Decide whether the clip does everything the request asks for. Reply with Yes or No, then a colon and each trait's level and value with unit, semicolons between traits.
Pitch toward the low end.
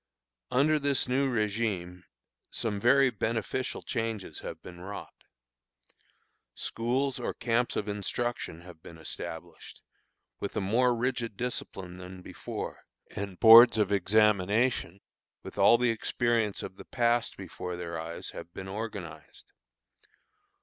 Yes: low, 110 Hz